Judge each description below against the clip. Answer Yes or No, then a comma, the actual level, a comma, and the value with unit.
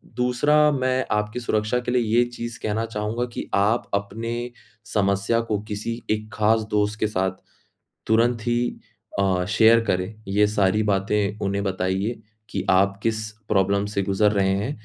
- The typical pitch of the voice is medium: No, low, 105 Hz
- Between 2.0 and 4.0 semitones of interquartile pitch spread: Yes, average, 2.7 semitones